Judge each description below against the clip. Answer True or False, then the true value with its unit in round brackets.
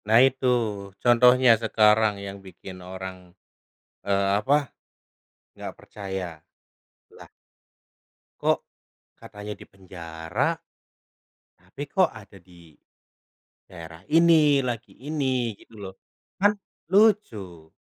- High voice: False (105 Hz)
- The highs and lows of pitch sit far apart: True (5.8 semitones)